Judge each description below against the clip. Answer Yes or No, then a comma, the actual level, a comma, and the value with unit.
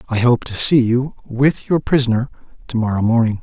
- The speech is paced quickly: No, average, 195 wpm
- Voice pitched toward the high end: No, low, 120 Hz